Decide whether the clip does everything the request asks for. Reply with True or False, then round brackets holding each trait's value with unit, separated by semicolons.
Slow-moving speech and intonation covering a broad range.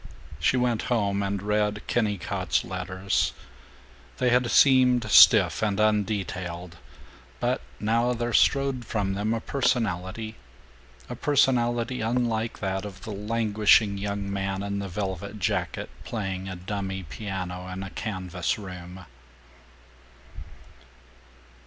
False (115 wpm; 3.3 semitones)